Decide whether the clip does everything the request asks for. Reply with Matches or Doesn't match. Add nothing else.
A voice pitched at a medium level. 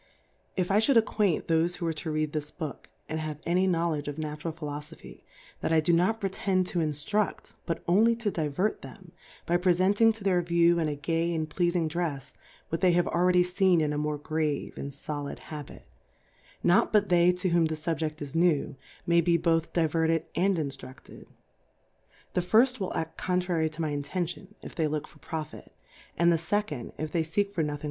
Matches